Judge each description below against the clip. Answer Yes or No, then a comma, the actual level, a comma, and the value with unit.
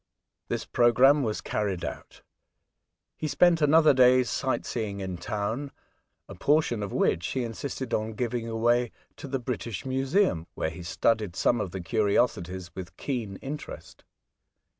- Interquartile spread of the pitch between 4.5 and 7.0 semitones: Yes, average, 4.9 semitones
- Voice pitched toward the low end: Yes, low, 115 Hz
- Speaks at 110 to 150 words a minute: Yes, average, 145 wpm